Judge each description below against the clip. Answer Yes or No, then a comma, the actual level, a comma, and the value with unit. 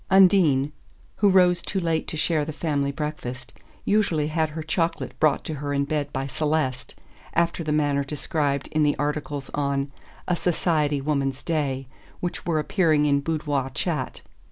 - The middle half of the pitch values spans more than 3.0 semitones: No, narrow, 2.6 semitones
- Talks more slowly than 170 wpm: Yes, average, 160 wpm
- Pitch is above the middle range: No, medium, 150 Hz